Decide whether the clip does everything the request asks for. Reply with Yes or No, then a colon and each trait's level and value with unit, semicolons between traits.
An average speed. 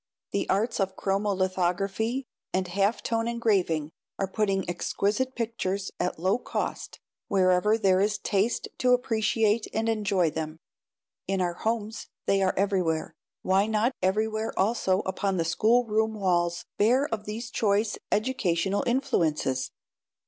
No: slow, 130 wpm